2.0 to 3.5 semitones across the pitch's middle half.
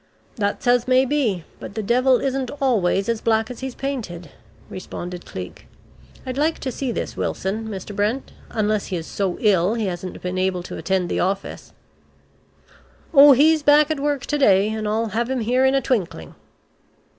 No: wide, 5.5 semitones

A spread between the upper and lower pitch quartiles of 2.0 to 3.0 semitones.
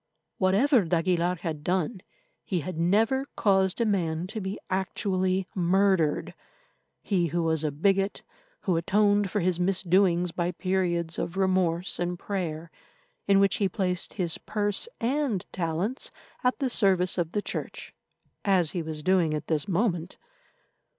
Yes: average, 2.7 semitones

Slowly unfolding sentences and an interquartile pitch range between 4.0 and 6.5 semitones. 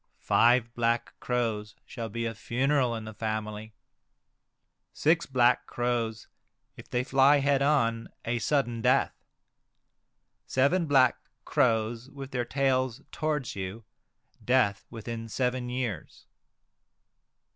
No: slow, 115 wpm; average, 2.9 semitones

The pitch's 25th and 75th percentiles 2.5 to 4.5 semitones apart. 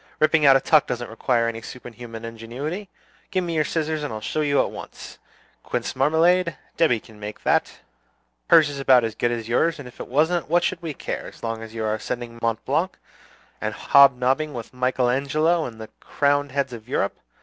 No: average, 5.0 semitones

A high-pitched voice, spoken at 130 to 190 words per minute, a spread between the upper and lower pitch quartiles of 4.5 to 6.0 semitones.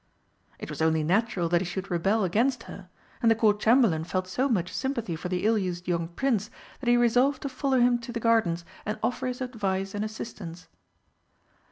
No: high, 210 Hz; average, 200 wpm; average, 5.2 semitones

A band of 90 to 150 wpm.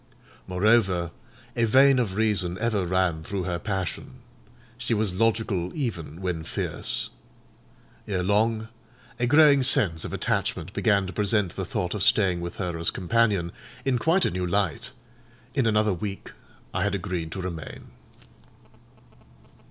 Yes: average, 145 wpm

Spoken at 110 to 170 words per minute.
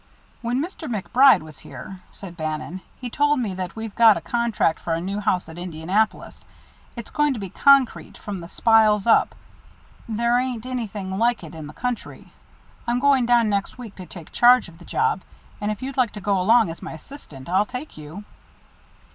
No: average, 195 wpm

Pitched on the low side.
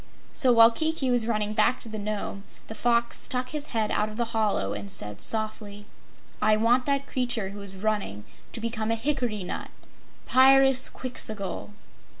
No: high, 225 Hz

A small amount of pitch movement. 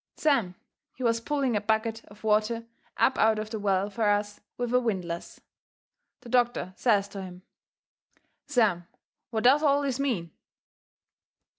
No: average, 3.3 semitones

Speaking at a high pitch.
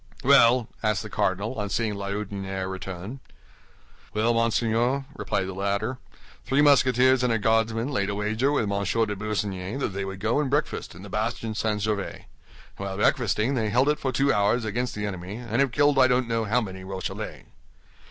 No: low, 110 Hz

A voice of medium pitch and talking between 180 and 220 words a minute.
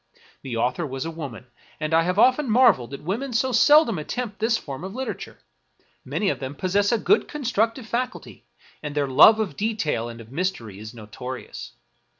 Yes: medium, 180 Hz; average, 190 wpm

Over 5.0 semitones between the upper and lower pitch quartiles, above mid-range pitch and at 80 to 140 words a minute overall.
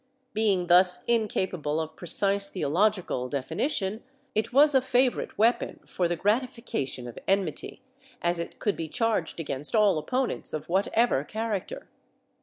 Yes: wide, 5.5 semitones; high, 195 Hz; slow, 135 wpm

